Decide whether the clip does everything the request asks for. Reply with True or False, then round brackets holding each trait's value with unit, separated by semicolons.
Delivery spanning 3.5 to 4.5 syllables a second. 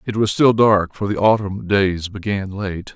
True (4.3 syllables/s)